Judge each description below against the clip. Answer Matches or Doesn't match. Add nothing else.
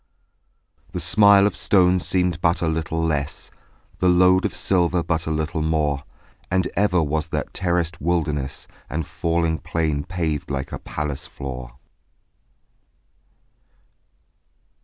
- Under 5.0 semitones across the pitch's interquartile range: Matches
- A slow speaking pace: Matches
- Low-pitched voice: Matches